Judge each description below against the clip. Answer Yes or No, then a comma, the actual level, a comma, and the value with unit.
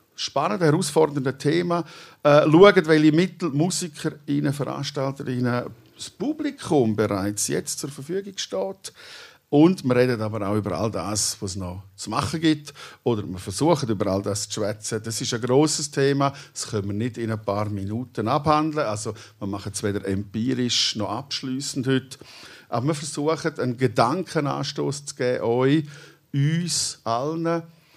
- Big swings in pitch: Yes, wide, 6.1 semitones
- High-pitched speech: No, low, 135 Hz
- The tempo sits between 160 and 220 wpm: No, average, 150 wpm